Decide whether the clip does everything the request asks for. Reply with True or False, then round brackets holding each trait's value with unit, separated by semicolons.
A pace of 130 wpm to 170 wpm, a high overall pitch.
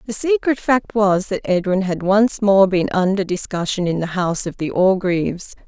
False (190 wpm; 195 Hz)